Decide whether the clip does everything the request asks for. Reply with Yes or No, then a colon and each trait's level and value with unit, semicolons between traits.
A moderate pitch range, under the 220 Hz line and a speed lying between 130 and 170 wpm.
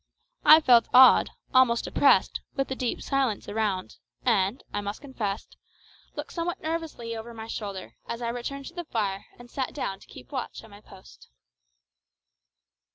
No: average, 4.7 semitones; high, 235 Hz; average, 160 wpm